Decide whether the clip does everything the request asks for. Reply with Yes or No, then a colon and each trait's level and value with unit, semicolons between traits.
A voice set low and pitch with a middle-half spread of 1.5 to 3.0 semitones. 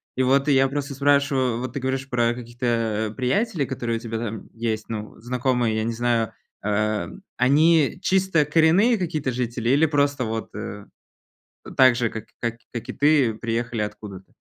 No: low, 125 Hz; average, 3.7 semitones